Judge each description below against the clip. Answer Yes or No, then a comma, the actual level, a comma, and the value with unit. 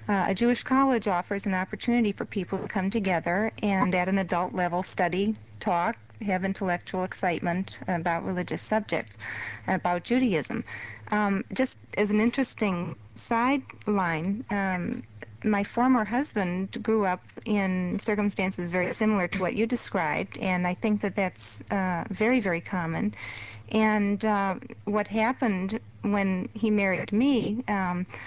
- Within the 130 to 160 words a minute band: Yes, average, 140 wpm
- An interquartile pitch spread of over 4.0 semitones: No, average, 3.2 semitones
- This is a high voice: Yes, high, 195 Hz